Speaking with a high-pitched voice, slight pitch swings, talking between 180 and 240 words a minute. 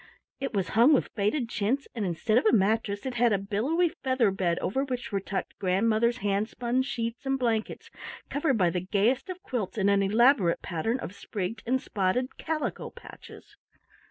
No: high, 225 Hz; average, 4.6 semitones; average, 185 wpm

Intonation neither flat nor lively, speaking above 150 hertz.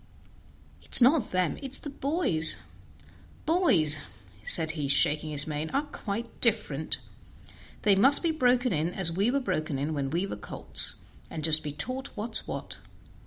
No: wide, 8.6 semitones; medium, 185 Hz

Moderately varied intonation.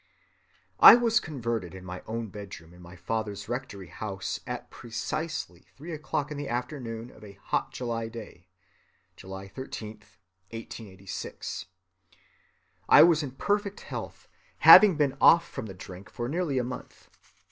No: wide, 6.8 semitones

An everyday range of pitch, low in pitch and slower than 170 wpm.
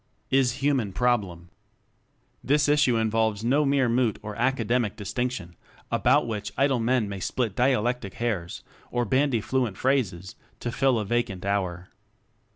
Yes: average, 4.1 semitones; low, 120 Hz; average, 140 wpm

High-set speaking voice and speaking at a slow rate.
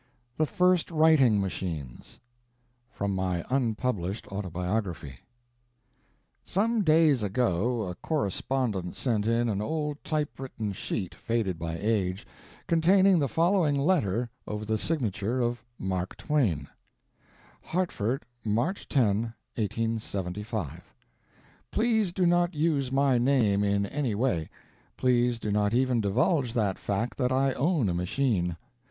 No: low, 115 Hz; slow, 120 wpm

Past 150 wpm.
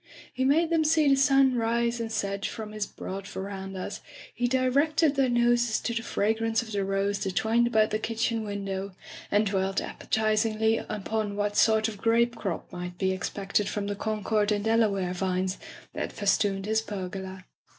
Yes: average, 175 wpm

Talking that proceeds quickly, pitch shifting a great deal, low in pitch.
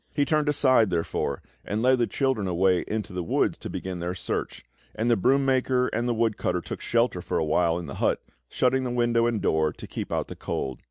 Yes: fast, 220 wpm; wide, 6.3 semitones; low, 110 Hz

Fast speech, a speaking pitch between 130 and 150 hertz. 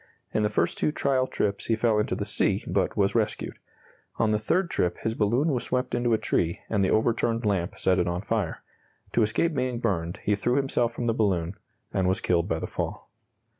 No: fast, 215 wpm; low, 110 Hz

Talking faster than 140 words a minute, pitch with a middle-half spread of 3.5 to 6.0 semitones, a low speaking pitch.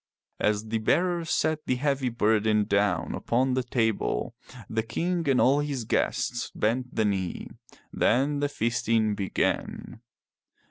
No: slow, 135 wpm; average, 4.5 semitones; low, 120 Hz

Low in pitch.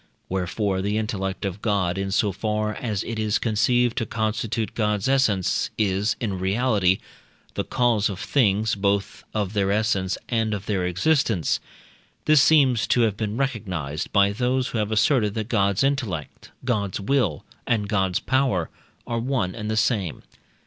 Yes: low, 105 Hz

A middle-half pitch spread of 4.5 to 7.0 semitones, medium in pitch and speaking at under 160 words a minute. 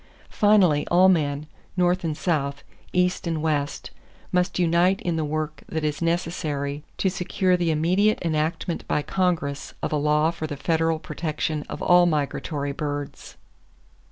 No: average, 3.0 semitones; medium, 160 Hz; average, 150 wpm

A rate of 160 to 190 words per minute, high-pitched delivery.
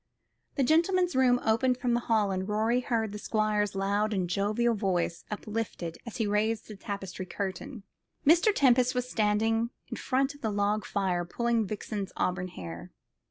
Yes: average, 165 wpm; high, 215 Hz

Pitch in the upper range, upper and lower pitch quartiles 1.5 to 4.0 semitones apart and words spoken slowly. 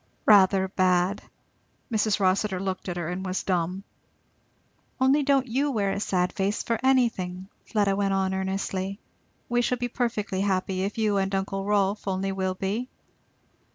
No: high, 195 Hz; narrow, 2.4 semitones; average, 155 wpm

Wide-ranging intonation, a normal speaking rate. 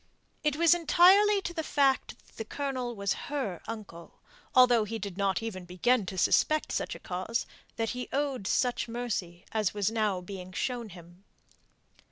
Yes: wide, 5.8 semitones; average, 170 wpm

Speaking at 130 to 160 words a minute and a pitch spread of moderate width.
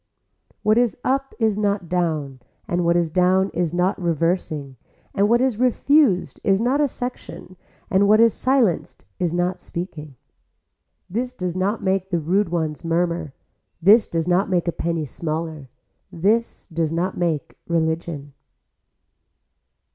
Yes: average, 145 wpm; average, 4.0 semitones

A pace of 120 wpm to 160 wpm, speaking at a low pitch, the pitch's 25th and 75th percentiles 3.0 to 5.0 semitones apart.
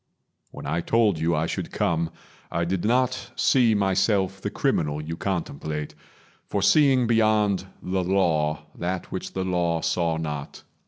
Yes: average, 150 wpm; very low, 90 Hz; average, 4.2 semitones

